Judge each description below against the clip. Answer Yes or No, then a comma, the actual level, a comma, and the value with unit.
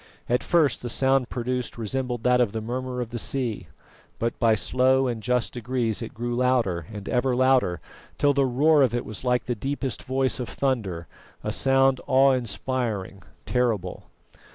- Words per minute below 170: No, average, 175 wpm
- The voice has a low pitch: Yes, low, 125 Hz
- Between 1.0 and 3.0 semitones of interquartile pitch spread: Yes, narrow, 2.5 semitones